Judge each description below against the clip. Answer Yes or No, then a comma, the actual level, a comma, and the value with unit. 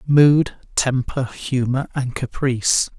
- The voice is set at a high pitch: No, low, 130 Hz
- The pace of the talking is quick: No, slow, 100 wpm